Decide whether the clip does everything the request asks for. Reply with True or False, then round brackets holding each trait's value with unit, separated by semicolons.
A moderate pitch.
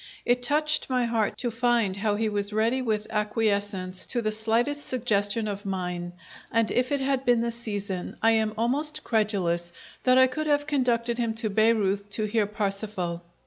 False (220 Hz)